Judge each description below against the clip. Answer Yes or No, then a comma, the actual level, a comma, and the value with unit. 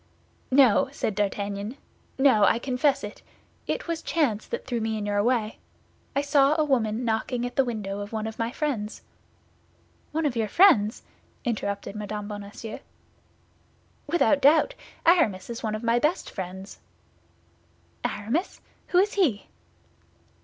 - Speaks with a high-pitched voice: Yes, high, 230 Hz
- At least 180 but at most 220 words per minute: No, average, 145 wpm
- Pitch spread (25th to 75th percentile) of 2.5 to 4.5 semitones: No, average, 5.2 semitones